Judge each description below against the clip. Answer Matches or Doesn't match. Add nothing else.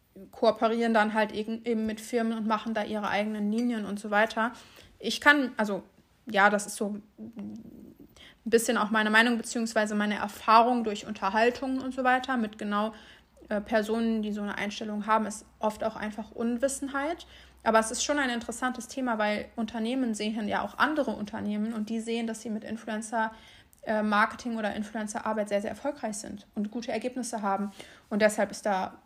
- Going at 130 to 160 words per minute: Doesn't match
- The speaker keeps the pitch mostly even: Matches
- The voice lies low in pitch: Doesn't match